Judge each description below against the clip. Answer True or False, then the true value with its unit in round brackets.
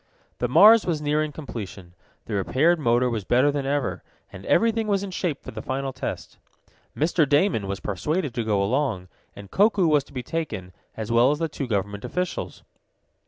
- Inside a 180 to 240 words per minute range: True (185 wpm)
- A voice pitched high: False (135 Hz)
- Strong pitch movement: True (6.8 semitones)